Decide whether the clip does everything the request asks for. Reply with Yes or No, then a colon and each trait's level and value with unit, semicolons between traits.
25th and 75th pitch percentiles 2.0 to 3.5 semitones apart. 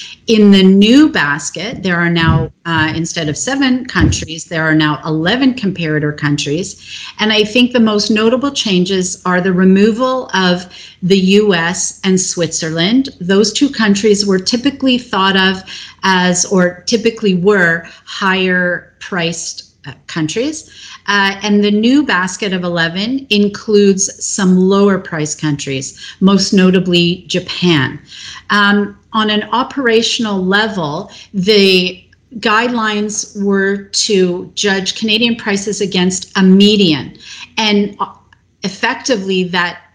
Yes: average, 3.2 semitones